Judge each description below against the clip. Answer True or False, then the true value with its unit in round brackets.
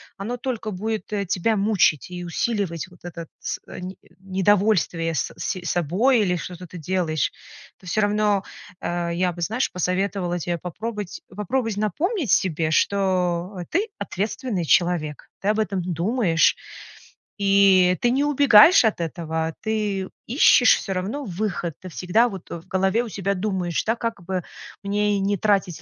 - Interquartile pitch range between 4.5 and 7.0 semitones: False (3.5 semitones)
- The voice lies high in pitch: True (195 Hz)